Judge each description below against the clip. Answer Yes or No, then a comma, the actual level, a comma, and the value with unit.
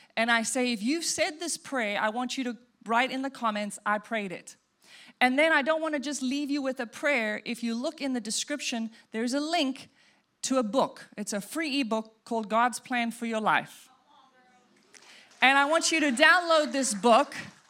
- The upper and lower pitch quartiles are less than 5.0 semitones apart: Yes, average, 4.1 semitones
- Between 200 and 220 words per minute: Yes, fast, 205 wpm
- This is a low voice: No, very high, 250 Hz